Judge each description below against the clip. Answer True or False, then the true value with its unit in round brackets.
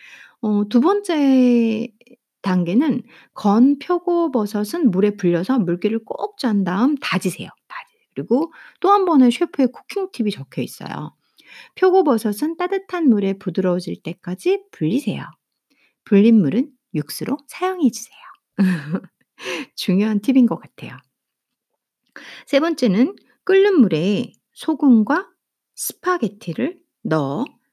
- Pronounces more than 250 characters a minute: False (240 characters per minute)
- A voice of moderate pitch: False (245 Hz)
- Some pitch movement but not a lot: False (7.1 semitones)